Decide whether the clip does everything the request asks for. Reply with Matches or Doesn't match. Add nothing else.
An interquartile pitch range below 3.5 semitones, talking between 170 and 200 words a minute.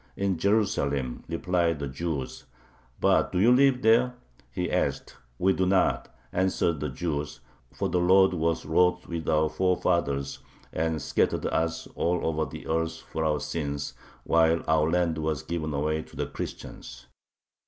Doesn't match